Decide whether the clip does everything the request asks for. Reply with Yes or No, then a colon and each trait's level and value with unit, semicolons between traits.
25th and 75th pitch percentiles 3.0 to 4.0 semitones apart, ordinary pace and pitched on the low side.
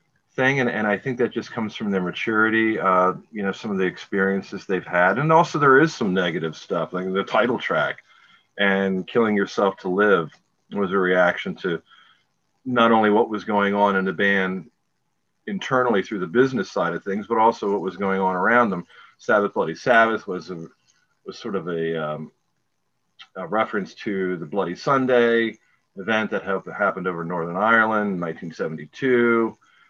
Yes: average, 3.3 semitones; average, 175 wpm; low, 100 Hz